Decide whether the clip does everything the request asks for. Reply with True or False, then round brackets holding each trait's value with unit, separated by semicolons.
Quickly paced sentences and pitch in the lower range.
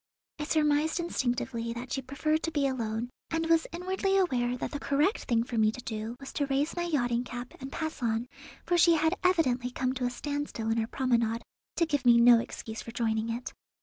False (215 wpm; 255 Hz)